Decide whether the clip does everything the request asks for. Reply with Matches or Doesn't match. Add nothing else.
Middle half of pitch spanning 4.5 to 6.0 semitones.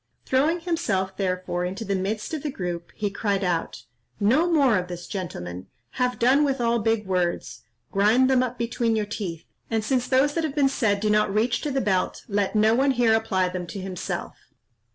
Matches